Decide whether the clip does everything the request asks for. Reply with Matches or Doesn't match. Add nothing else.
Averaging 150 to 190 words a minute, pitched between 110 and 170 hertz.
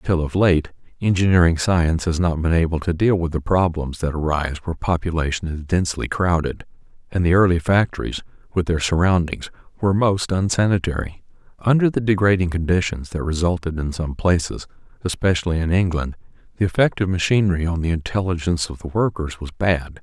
Doesn't match